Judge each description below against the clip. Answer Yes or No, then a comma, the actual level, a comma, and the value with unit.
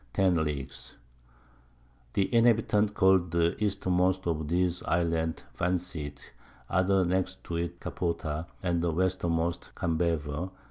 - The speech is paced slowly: Yes, slow, 125 wpm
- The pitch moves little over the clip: Yes, narrow, 2.3 semitones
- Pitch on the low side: Yes, very low, 85 Hz